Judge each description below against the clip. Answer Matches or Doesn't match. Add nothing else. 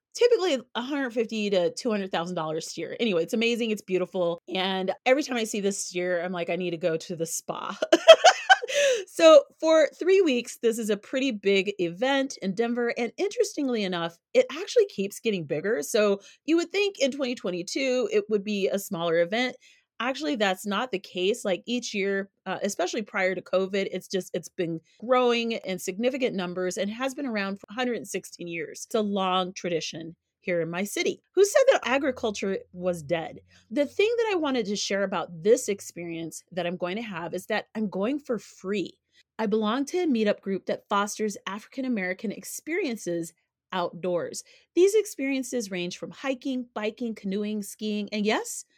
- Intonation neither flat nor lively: Doesn't match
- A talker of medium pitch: Doesn't match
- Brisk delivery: Doesn't match